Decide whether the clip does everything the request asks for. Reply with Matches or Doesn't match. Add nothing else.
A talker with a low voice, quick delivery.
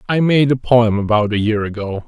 Matches